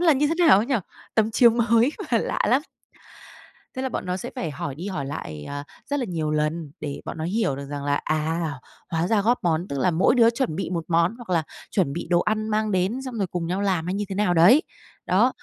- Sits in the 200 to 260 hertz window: No, medium, 185 Hz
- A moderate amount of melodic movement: No, wide, 6.0 semitones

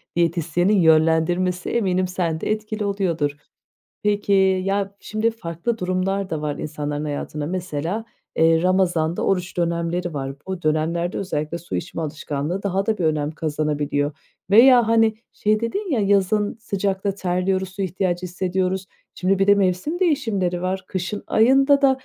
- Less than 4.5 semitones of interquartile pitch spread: Yes, average, 3.6 semitones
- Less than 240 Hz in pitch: Yes, medium, 185 Hz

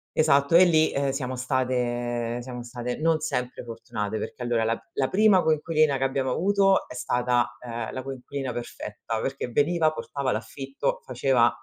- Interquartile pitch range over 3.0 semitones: Yes, average, 4.1 semitones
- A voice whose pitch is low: Yes, low, 130 Hz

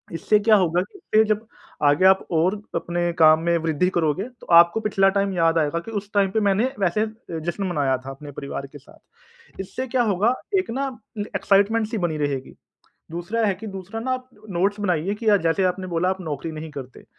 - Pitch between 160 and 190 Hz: Yes, medium, 185 Hz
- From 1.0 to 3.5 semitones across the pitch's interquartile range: No, average, 4.2 semitones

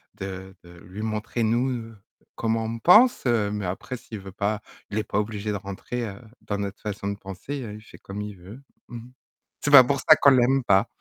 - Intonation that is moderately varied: Yes, average, 3.3 semitones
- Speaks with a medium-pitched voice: No, low, 110 Hz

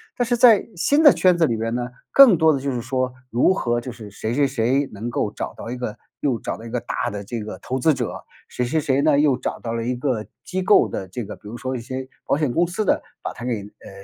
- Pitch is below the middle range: Yes, low, 125 Hz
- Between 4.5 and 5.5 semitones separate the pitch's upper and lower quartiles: Yes, average, 4.8 semitones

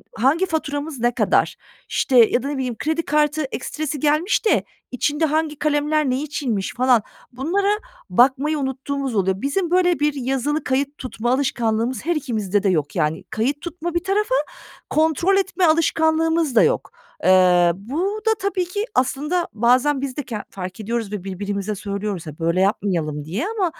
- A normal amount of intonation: No, wide, 6.5 semitones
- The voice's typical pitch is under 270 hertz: No, very high, 275 Hz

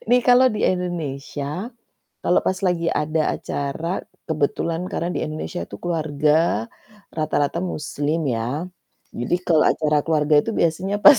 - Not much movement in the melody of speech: No, average, 3.0 semitones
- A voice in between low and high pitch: Yes, medium, 160 Hz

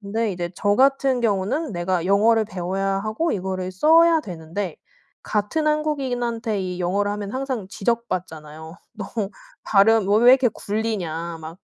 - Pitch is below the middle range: No, high, 205 Hz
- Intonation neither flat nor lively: Yes, average, 4.6 semitones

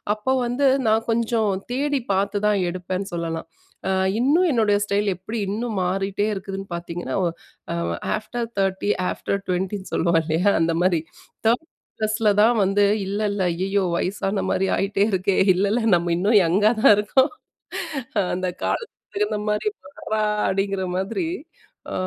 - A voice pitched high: Yes, high, 200 Hz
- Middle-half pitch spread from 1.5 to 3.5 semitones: Yes, average, 2.8 semitones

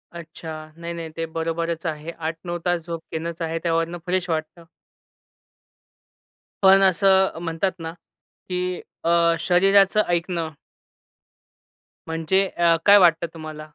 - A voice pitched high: No, medium, 170 Hz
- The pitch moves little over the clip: Yes, narrow, 1.8 semitones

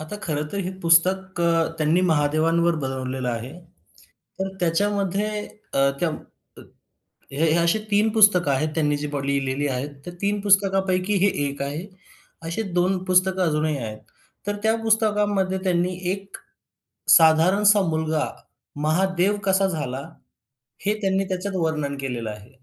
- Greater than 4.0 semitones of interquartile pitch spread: Yes, average, 4.6 semitones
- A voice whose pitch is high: No, medium, 170 Hz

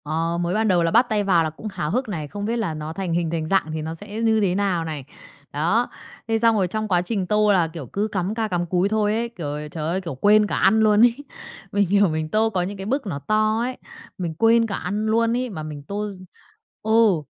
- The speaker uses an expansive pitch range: No, average, 4.6 semitones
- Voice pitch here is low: No, high, 200 Hz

